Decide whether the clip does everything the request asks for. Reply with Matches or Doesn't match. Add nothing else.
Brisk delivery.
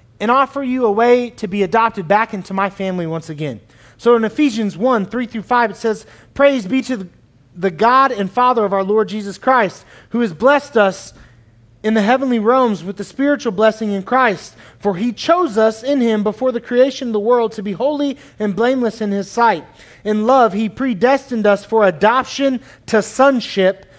Doesn't match